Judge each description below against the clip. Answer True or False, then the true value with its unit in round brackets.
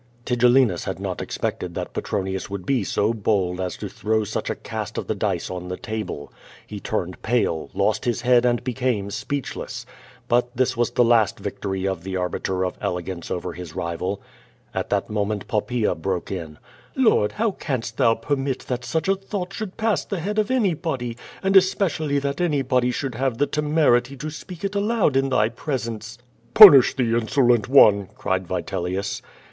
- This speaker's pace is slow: False (175 wpm)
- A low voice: True (120 Hz)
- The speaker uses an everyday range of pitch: False (6.4 semitones)